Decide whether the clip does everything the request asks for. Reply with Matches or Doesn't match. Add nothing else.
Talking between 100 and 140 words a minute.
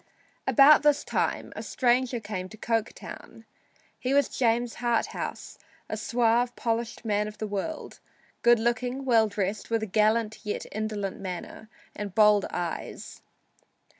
Matches